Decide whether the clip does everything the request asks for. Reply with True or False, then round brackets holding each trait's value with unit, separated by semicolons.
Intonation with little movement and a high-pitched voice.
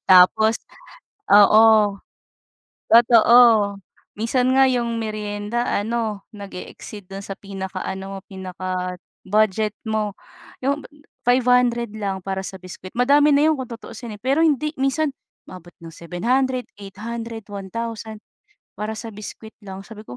False (3.5 semitones; 215 Hz)